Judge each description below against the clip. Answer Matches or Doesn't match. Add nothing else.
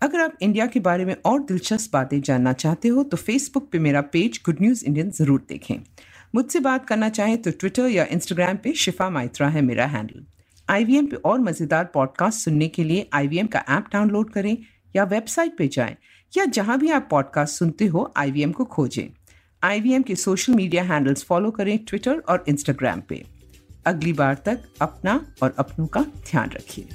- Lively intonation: Matches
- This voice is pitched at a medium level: Matches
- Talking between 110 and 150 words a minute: Doesn't match